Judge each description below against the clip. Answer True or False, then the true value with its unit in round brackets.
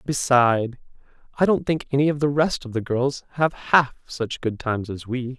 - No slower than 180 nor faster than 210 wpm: True (200 wpm)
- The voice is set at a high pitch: False (130 Hz)